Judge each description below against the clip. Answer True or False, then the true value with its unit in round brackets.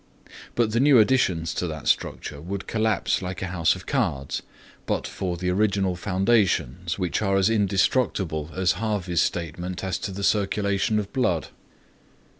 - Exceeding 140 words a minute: True (160 wpm)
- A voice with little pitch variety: False (3.2 semitones)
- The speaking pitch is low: True (95 Hz)